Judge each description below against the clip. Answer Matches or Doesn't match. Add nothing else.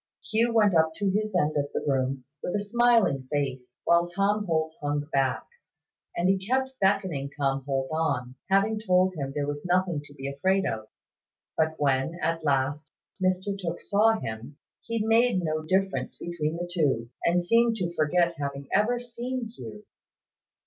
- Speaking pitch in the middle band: Matches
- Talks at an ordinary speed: Matches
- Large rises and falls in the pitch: Matches